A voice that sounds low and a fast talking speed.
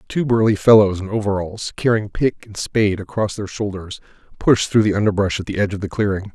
Yes: low, 100 Hz; fast, 210 wpm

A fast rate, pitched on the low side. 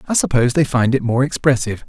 Yes: fast, 225 wpm; low, 130 Hz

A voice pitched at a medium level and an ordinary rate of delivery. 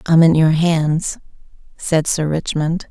Yes: medium, 160 Hz; average, 145 wpm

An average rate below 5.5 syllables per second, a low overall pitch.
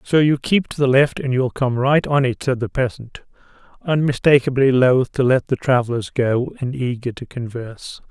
Yes: 4.9 syllables/s; low, 130 Hz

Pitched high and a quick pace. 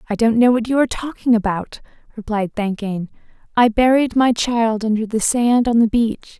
No: high, 230 Hz; average, 190 wpm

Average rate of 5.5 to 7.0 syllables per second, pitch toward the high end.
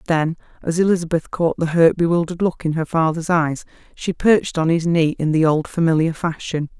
No: 5.6 syllables/s; medium, 165 Hz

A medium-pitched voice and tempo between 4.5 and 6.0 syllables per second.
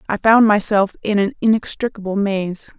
No: high, 205 Hz; 4.9 syllables/s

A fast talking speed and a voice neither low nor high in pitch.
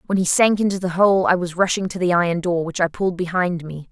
Yes: fast, 275 wpm; medium, 180 Hz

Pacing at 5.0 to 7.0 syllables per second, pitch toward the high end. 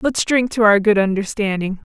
Yes: 5.1 syllables/s; high, 210 Hz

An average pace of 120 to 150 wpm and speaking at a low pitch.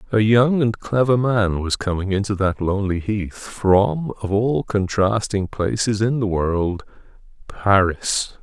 Yes: average, 140 wpm; low, 105 Hz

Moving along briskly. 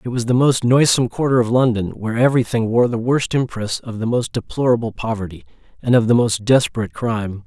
Yes: fast, 210 wpm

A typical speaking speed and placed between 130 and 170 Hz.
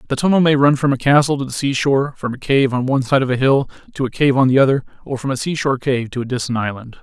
No: fast, 290 wpm; low, 135 Hz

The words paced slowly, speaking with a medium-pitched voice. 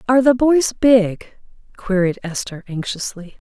No: slow, 120 wpm; high, 215 Hz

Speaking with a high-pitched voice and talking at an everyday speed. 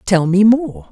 Yes: high, 195 Hz; average, 195 wpm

